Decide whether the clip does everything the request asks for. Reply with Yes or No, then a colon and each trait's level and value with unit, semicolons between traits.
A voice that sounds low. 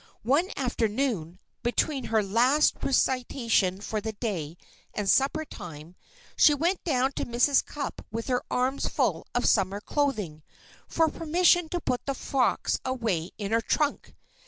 No: high, 245 Hz